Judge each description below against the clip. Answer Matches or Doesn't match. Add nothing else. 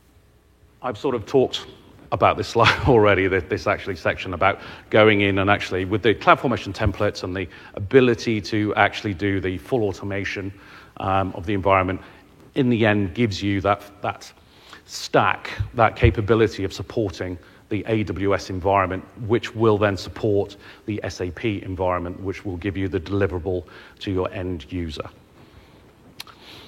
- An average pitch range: Doesn't match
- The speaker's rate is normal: Matches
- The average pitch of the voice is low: Matches